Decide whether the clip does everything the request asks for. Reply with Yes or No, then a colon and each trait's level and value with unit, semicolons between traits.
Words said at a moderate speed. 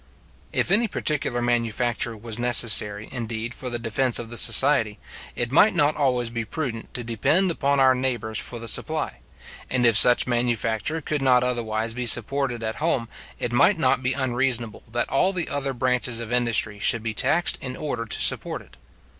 Yes: average, 180 wpm